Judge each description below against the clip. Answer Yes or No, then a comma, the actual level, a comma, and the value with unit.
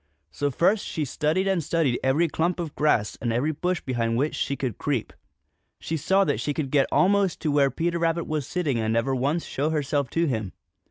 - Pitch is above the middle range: No, medium, 150 Hz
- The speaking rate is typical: No, fast, 210 wpm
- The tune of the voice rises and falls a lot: No, average, 4.1 semitones